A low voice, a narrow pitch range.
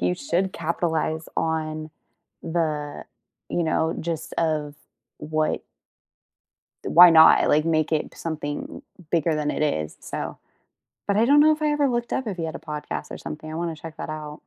No: medium, 160 Hz; narrow, 1.9 semitones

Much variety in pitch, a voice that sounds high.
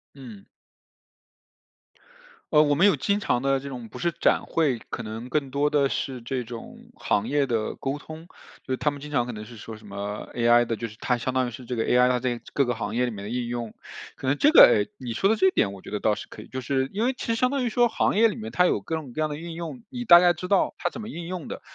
No: wide, 6.4 semitones; low, 135 Hz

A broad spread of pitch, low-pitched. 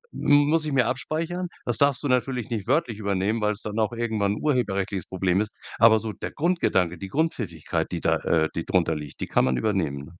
Yes: wide, 5.9 semitones; low, 110 Hz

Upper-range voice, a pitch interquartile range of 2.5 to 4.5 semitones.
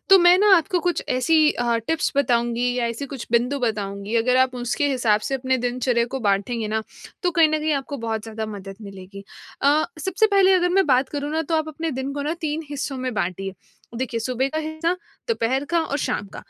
No: very high, 260 Hz; average, 5.3 semitones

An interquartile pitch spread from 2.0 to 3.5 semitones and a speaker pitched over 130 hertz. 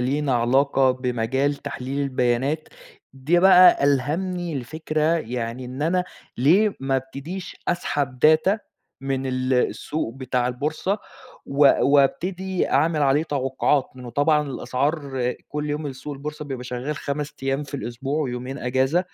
Yes: average, 2.9 semitones; medium, 140 Hz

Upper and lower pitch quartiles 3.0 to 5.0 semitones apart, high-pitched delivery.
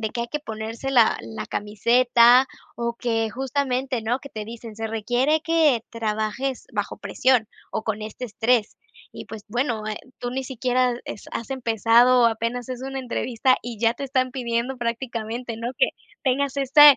No: narrow, 2.5 semitones; high, 240 Hz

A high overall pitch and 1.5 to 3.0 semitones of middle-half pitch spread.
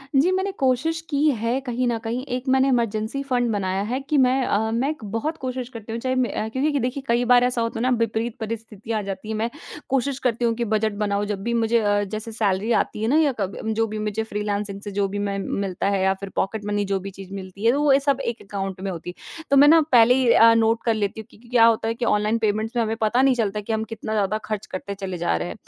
No: high, 225 Hz; average, 3.4 semitones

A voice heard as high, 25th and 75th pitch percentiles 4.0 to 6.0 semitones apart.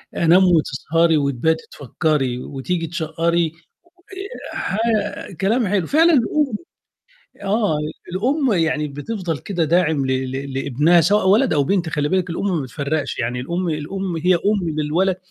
No: medium, 165 Hz; average, 4.3 semitones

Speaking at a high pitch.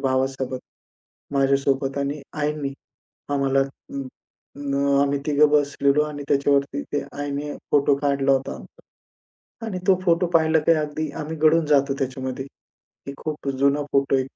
No: medium, 140 Hz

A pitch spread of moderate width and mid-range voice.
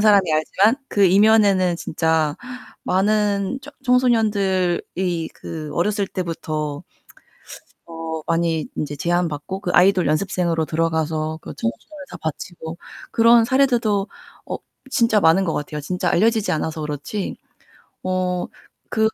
Yes: average, 4.4 semitones; medium, 180 Hz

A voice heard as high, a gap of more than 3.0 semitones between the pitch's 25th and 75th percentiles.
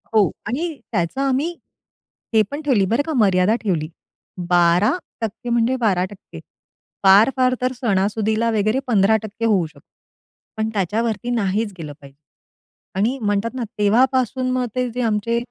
Yes: high, 220 Hz; average, 4.0 semitones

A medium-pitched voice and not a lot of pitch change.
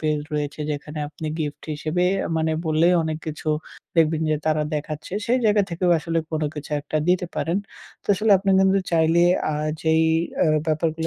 Yes: medium, 160 Hz; narrow, 1.8 semitones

